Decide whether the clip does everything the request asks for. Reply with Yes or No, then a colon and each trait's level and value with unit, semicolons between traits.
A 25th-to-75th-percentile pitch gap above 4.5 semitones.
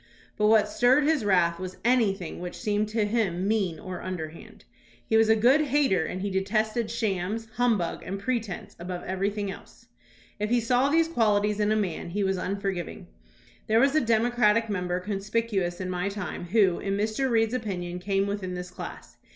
No: average, 3.5 semitones